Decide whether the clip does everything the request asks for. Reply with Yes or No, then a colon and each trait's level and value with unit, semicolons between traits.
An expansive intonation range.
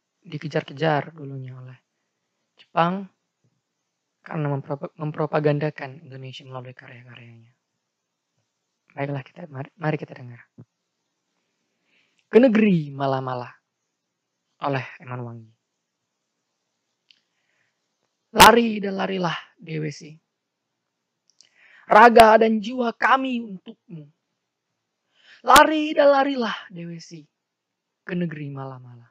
Yes: wide, 6.7 semitones